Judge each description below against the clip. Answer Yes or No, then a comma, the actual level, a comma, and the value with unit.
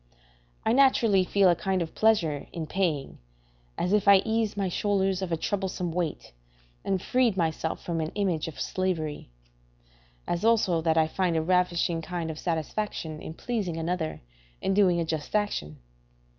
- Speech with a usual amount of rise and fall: Yes, average, 3.7 semitones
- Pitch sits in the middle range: Yes, medium, 180 Hz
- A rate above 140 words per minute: Yes, average, 165 wpm